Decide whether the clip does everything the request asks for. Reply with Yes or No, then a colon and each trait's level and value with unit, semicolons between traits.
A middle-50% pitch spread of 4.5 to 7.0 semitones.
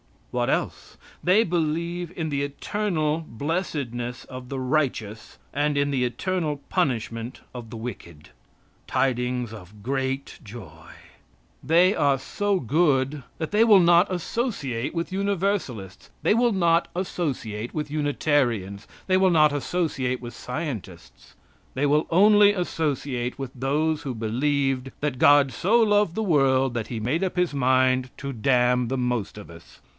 Yes: wide, 5.5 semitones